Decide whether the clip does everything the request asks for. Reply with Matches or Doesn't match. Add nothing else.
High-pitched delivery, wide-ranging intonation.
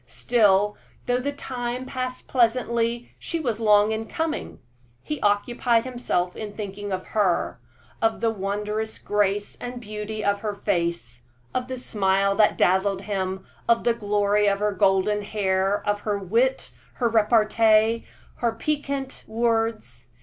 Doesn't match